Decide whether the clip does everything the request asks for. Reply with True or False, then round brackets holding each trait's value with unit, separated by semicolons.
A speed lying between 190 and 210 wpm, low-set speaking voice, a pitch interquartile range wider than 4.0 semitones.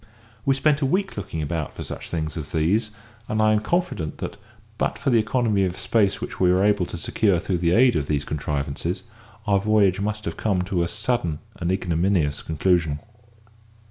True (195 wpm; 95 Hz; 4.6 semitones)